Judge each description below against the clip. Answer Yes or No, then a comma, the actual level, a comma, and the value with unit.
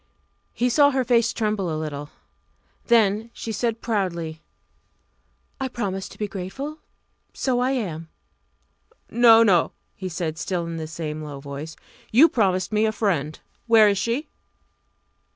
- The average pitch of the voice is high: Yes, high, 200 Hz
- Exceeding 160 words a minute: No, average, 145 wpm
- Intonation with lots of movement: Yes, wide, 6.0 semitones